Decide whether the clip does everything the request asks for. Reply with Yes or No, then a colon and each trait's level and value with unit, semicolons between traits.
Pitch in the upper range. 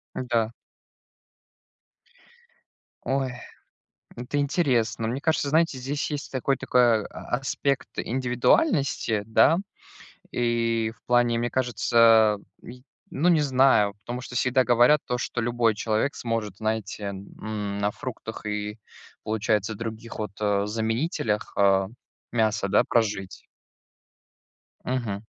No: low, 115 Hz